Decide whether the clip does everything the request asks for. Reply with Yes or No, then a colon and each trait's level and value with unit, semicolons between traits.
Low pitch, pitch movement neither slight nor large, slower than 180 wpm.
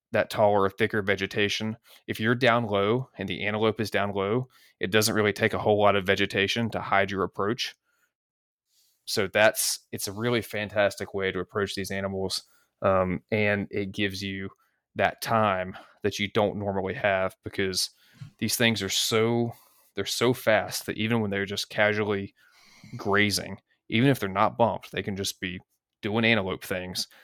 No: low, 100 Hz; narrow, 2.1 semitones; average, 170 wpm